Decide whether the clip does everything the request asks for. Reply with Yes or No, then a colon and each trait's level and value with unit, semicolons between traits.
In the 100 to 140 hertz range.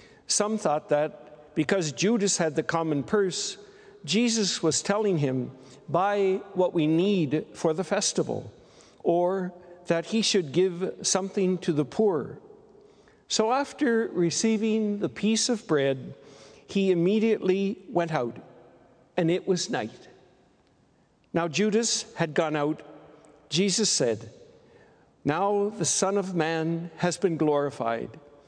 No: medium, 180 Hz